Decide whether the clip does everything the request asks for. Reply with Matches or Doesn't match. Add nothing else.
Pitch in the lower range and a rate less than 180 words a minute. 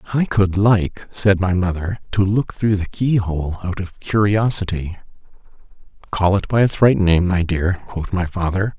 Matches